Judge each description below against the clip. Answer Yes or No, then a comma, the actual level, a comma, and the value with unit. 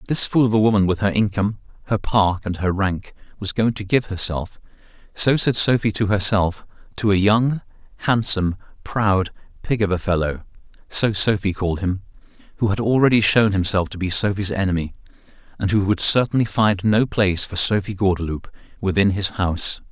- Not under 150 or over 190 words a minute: Yes, average, 165 wpm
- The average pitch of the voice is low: Yes, low, 100 Hz